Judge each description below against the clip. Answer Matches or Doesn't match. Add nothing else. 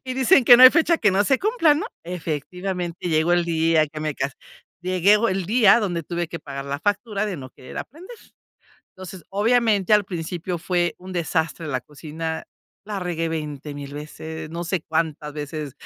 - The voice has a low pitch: Doesn't match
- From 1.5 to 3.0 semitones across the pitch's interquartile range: Doesn't match